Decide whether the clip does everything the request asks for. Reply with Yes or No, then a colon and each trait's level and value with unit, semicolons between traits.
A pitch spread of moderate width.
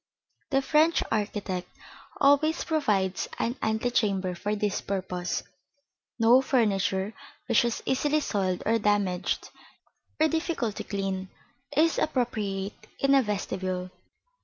No: wide, 5.8 semitones